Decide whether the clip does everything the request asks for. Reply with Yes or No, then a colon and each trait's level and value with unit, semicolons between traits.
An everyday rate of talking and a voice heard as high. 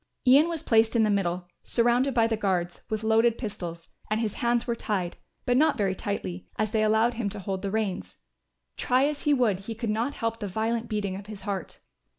No: fast, 215 wpm; high, 220 Hz